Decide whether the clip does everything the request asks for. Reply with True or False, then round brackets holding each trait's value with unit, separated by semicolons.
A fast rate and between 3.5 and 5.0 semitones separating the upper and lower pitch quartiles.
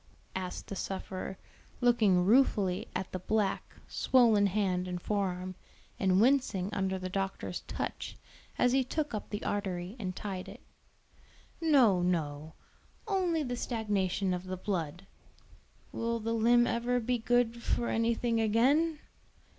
False (140 wpm; 4.5 semitones)